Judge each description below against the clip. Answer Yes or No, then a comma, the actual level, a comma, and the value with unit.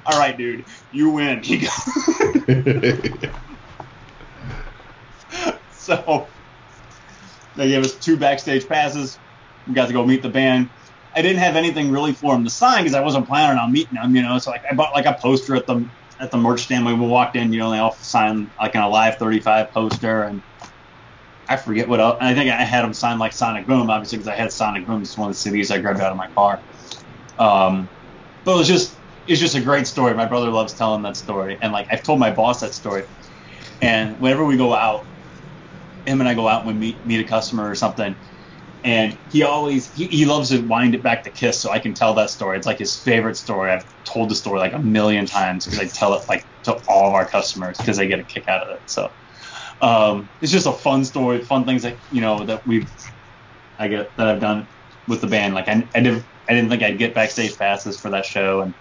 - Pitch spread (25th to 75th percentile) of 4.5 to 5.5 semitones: No, average, 3.7 semitones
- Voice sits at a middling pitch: No, low, 120 Hz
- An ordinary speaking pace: No, fast, 230 wpm